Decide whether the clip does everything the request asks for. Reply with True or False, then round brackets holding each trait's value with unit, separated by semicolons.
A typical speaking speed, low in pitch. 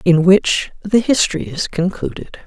False (145 wpm; 185 Hz)